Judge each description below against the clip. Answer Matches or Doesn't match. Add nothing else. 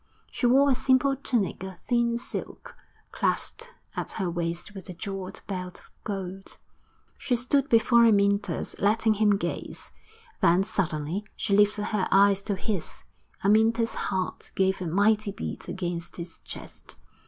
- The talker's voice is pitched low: Doesn't match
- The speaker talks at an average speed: Matches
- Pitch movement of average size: Matches